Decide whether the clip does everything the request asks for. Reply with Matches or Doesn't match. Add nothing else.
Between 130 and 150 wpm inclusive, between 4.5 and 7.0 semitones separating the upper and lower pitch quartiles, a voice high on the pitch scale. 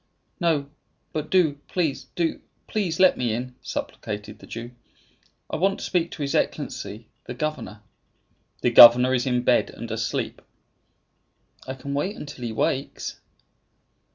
Doesn't match